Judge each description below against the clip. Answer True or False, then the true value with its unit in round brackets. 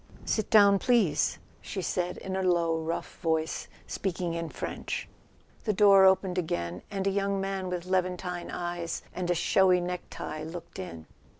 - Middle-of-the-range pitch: True (180 Hz)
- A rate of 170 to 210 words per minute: False (160 wpm)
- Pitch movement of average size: False (2.3 semitones)